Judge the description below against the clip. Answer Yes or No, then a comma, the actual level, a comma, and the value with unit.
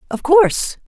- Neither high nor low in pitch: No, very high, 285 Hz